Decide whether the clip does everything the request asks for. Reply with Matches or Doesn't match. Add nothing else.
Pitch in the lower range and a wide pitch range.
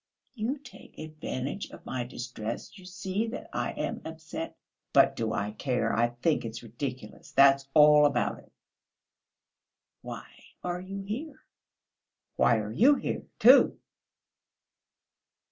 Doesn't match